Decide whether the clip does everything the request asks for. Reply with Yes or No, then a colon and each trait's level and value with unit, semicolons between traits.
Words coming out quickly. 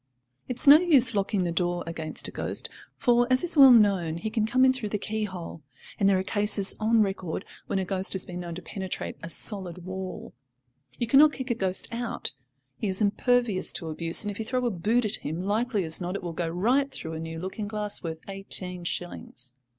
Yes: fast, 225 wpm